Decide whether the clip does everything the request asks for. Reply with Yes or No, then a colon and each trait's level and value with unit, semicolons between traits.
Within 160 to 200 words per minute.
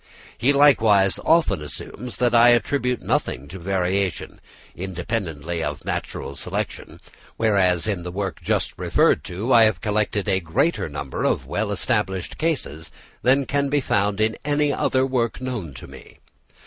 No: average, 150 wpm